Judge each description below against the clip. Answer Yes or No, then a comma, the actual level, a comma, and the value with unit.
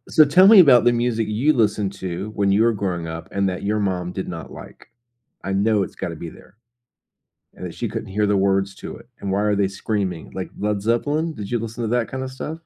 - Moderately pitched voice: No, low, 105 Hz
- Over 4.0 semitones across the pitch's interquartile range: No, average, 3.5 semitones